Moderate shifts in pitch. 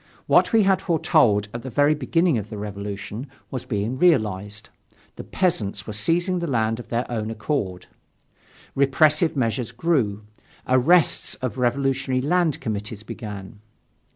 No: wide, 6.0 semitones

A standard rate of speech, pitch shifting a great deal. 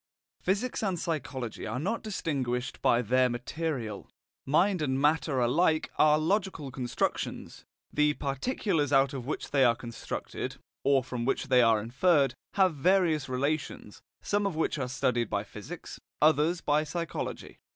No: average, 145 wpm; average, 4.7 semitones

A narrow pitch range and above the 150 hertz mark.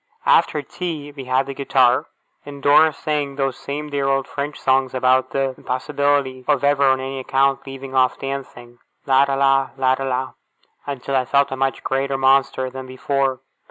No: narrow, 1.2 semitones; low, 135 Hz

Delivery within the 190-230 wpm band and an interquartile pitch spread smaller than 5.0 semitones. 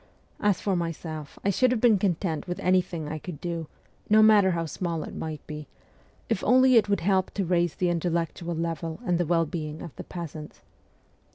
Yes: average, 200 wpm; average, 2.9 semitones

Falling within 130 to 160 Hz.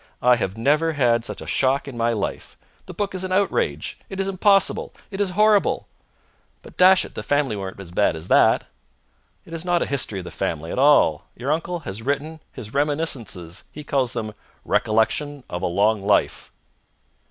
Yes: low, 135 Hz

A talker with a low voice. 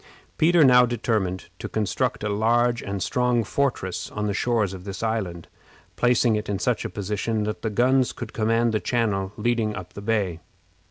Yes: low, 110 Hz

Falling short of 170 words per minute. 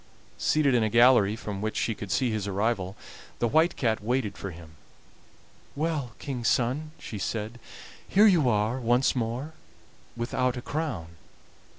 Yes: average, 155 wpm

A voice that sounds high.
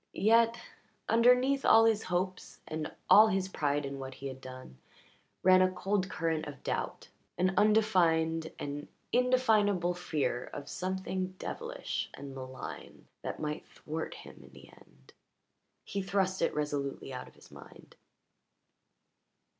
No: medium, 180 Hz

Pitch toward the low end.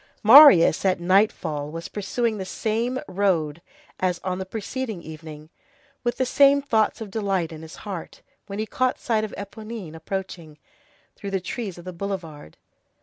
No: high, 195 Hz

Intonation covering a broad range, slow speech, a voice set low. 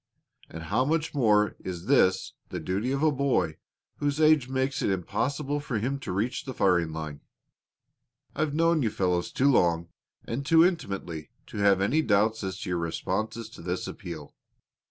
No: wide, 7.5 semitones; average, 175 wpm; low, 110 Hz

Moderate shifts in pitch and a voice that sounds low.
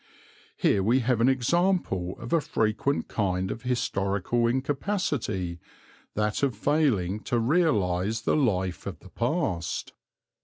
No: wide, 6.1 semitones; low, 115 Hz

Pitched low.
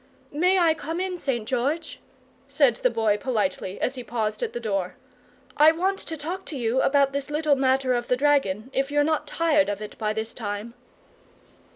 No: very high, 265 Hz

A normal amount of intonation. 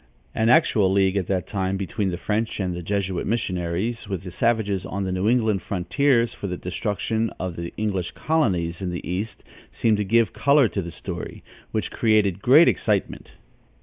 Yes: average, 3.4 semitones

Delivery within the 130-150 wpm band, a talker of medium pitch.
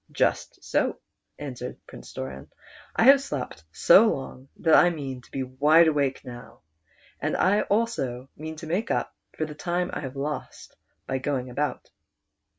No: average, 160 wpm; medium, 145 Hz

